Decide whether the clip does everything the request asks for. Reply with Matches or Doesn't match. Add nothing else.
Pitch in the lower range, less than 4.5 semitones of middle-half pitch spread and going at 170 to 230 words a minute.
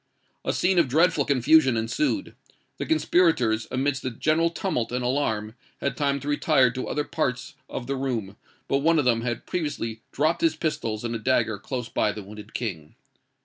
Doesn't match